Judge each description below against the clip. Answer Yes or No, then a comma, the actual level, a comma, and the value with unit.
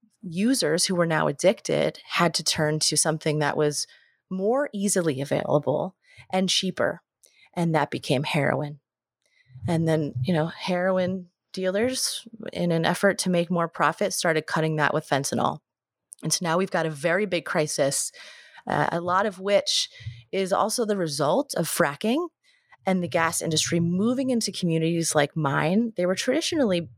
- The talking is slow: No, average, 160 wpm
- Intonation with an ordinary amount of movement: Yes, average, 4.5 semitones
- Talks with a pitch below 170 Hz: No, medium, 175 Hz